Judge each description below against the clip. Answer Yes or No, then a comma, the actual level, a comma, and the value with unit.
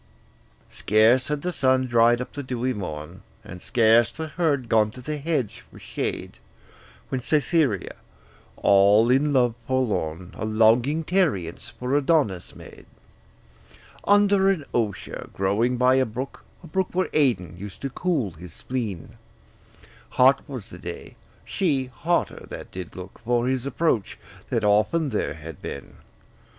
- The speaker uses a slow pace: No, average, 145 wpm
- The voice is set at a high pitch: No, low, 125 Hz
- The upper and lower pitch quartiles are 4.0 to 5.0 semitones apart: No, wide, 5.6 semitones